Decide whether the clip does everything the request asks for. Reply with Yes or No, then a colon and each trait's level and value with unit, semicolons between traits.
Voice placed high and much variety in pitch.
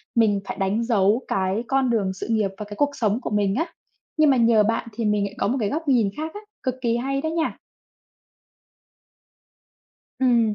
No: high, 230 Hz; average, 4.3 semitones